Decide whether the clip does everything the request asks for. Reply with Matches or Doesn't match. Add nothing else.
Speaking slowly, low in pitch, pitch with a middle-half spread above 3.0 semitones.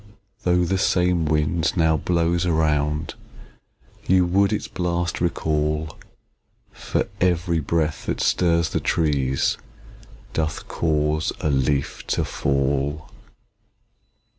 Doesn't match